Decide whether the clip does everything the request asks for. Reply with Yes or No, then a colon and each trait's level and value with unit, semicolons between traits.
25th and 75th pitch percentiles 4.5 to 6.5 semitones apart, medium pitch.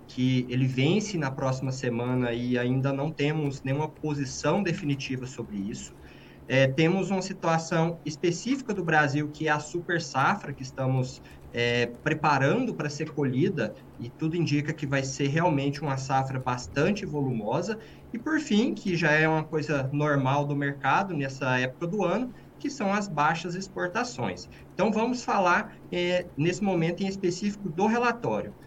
Yes: average, 5.0 semitones; medium, 150 Hz